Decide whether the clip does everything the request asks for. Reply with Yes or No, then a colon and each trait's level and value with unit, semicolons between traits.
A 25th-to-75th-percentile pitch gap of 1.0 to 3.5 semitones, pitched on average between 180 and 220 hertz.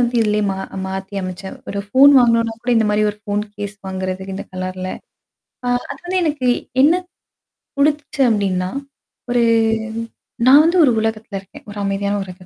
No: average, 4.5 semitones; high, 210 Hz